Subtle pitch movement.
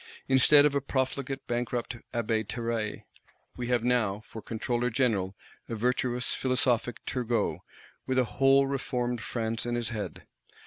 Yes: narrow, 2.1 semitones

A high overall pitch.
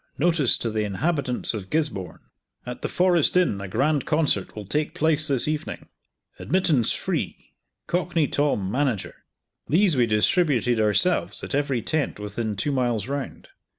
No: medium, 140 Hz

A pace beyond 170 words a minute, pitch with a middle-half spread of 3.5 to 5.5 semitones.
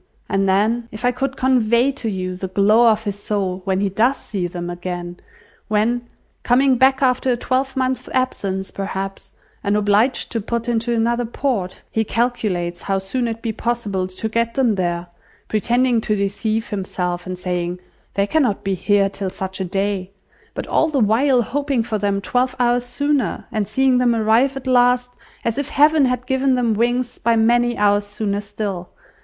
Yes: average, 180 wpm; average, 4.0 semitones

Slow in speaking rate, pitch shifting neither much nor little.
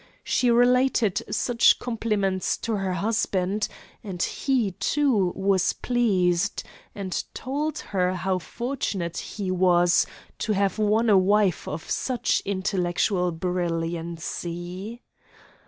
Yes: slow, 105 wpm; average, 4.1 semitones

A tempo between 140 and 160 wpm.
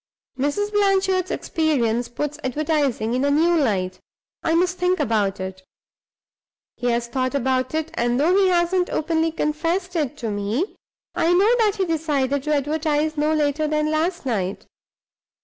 Yes: average, 155 wpm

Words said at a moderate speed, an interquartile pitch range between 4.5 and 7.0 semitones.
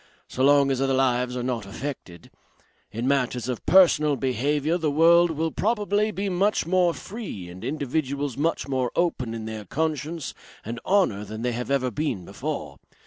Yes: average, 170 wpm; average, 5.0 semitones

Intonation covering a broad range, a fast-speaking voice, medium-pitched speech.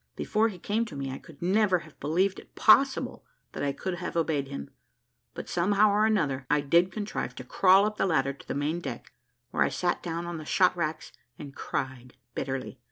Yes: wide, 5.7 semitones; fast, 210 wpm; medium, 170 Hz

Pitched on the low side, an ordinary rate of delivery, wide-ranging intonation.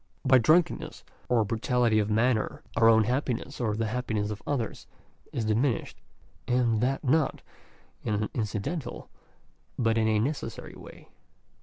No: low, 115 Hz; average, 155 wpm; average, 2.8 semitones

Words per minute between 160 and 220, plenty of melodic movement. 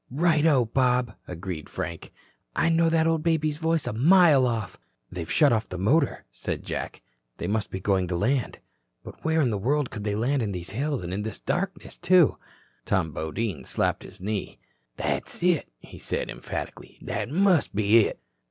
Yes: average, 180 wpm; wide, 7.9 semitones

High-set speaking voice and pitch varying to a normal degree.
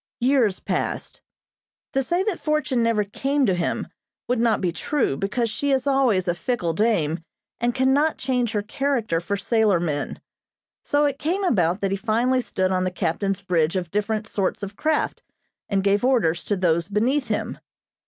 No: high, 215 Hz; wide, 5.8 semitones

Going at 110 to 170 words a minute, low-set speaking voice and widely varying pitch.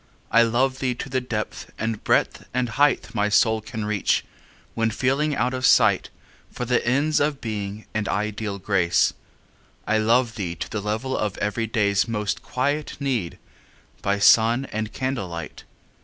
No: average, 155 wpm; low, 115 Hz; average, 3.5 semitones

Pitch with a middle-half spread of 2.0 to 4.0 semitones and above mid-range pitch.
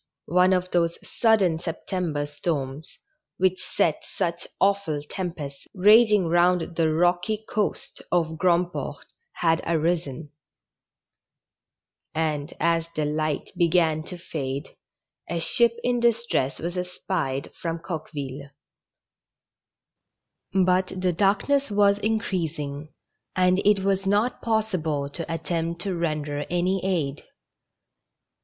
No: average, 3.4 semitones; medium, 175 Hz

